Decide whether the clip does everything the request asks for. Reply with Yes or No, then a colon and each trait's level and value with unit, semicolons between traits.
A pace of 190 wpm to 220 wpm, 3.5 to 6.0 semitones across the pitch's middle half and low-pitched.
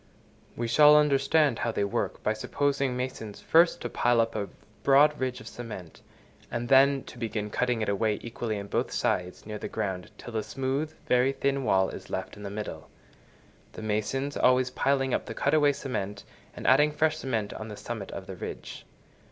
Yes: average, 195 wpm; average, 4.3 semitones; low, 125 Hz